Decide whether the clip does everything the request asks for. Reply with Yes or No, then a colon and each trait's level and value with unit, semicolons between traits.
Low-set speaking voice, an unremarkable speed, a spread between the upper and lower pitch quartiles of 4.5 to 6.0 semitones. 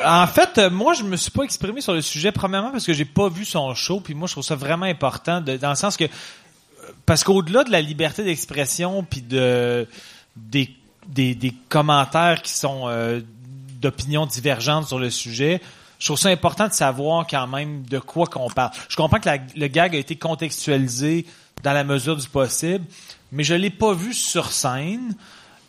No: medium, 155 Hz; average, 200 wpm; average, 4.9 semitones